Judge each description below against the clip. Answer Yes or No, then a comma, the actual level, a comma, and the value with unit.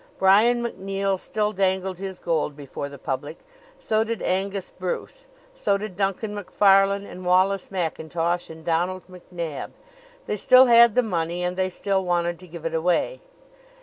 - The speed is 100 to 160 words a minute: Yes, average, 155 wpm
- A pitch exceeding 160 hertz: Yes, medium, 185 Hz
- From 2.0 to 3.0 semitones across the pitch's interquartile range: Yes, narrow, 2.6 semitones